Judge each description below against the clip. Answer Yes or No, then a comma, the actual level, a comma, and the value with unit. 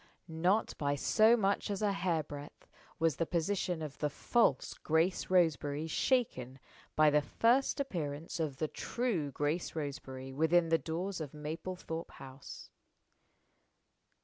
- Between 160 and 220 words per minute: No, slow, 135 wpm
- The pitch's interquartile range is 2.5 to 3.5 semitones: No, average, 4.2 semitones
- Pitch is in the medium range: Yes, medium, 160 Hz